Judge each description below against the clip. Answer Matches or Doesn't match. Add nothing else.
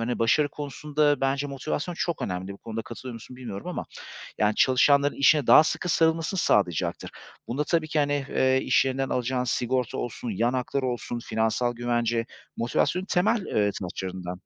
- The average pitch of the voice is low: Matches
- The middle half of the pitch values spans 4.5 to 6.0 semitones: Doesn't match